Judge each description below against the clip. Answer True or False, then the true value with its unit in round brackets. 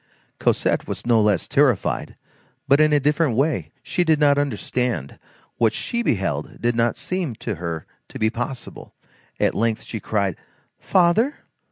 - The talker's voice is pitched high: False (120 Hz)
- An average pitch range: False (5.8 semitones)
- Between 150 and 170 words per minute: True (155 wpm)